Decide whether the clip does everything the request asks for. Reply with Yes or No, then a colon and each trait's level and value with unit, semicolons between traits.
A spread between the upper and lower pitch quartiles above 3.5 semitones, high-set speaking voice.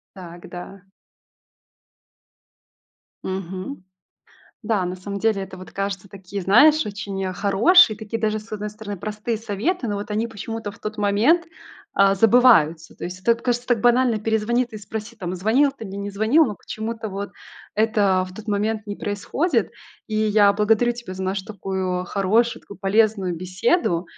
No: average, 2.7 semitones; high, 210 Hz